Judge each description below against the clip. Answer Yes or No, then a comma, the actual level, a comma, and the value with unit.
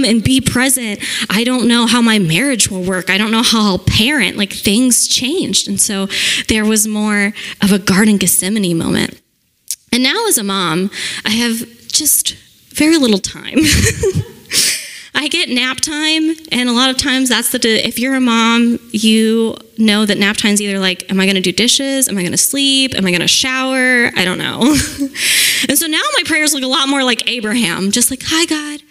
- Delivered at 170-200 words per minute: Yes, average, 195 wpm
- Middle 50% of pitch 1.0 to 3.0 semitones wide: No, average, 4.5 semitones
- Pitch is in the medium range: No, high, 235 Hz